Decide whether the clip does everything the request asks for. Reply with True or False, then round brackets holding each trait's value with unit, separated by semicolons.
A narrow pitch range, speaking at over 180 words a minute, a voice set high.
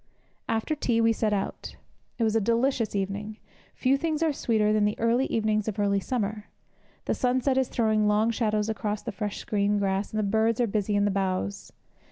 True (2.1 semitones; 200 wpm; 215 Hz)